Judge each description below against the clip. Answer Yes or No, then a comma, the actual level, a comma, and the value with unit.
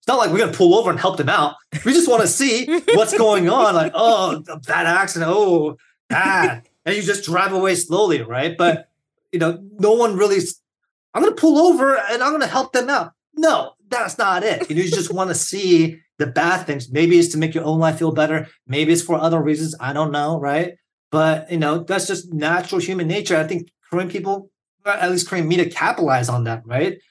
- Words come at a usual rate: No, fast, 225 wpm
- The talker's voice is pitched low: No, medium, 175 Hz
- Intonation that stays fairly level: No, average, 3.8 semitones